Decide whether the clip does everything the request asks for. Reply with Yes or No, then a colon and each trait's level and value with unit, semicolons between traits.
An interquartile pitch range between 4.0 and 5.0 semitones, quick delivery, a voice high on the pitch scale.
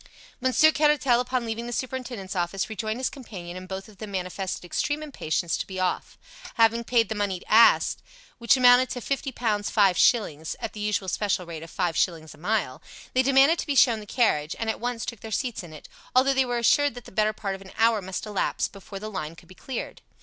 Yes: average, 4.7 semitones; fast, 225 wpm; high, 220 Hz